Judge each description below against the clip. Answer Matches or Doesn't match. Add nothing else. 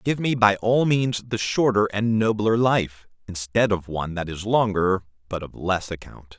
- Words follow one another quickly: Doesn't match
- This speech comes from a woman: Doesn't match